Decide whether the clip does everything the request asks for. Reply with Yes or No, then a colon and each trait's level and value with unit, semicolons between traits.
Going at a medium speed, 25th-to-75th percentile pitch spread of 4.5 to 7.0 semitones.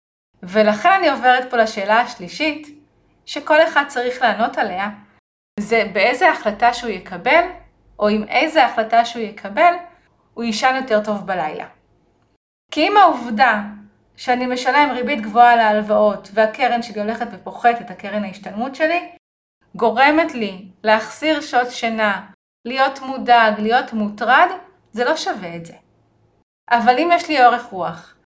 Yes: average, 130 wpm; average, 5.0 semitones